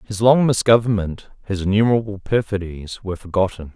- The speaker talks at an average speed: No, slow, 130 wpm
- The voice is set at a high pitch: No, low, 100 Hz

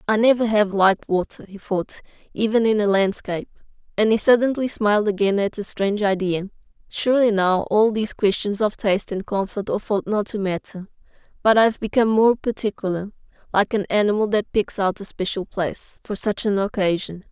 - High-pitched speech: Yes, high, 205 Hz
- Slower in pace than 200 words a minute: Yes, average, 175 wpm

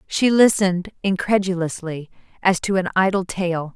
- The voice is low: No, medium, 185 Hz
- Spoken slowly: Yes, slow, 130 wpm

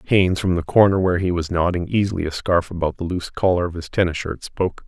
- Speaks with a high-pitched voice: No, very low, 90 Hz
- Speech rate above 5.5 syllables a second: Yes, 6.5 syllables/s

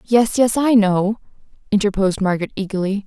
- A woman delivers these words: Yes, female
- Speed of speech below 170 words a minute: Yes, slow, 135 wpm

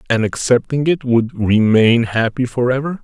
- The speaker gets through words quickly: No, average, 160 wpm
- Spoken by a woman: No, male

